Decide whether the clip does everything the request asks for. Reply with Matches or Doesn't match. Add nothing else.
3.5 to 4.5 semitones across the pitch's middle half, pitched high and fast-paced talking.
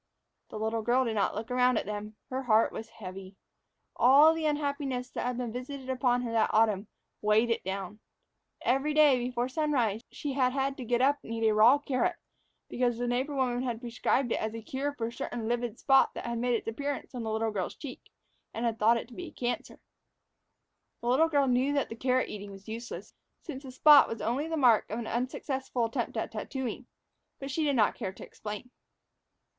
Doesn't match